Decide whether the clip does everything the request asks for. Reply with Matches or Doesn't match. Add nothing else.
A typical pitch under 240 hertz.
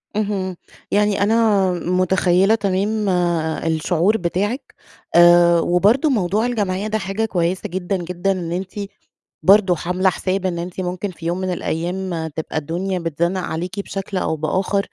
Matches